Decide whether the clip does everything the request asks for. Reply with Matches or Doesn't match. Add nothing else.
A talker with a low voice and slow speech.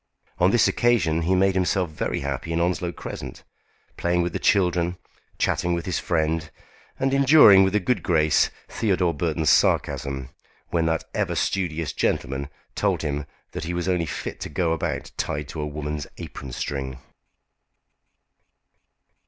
Doesn't match